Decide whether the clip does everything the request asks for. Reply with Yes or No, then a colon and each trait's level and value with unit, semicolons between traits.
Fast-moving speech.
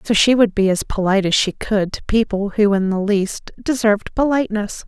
Yes: fast, 210 wpm